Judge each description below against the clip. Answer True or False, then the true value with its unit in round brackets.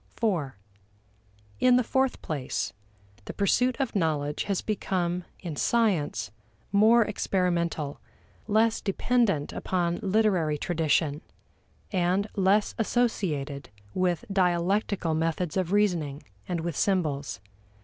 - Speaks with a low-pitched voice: False (180 Hz)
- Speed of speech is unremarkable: False (105 wpm)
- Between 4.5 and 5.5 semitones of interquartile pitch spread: True (4.8 semitones)